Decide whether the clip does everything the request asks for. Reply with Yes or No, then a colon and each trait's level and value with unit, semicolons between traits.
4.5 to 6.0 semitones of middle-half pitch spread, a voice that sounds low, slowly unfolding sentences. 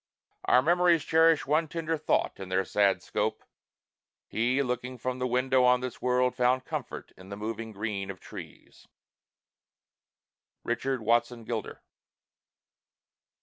No: average, 3.0 semitones; low, 125 Hz; slow, 130 wpm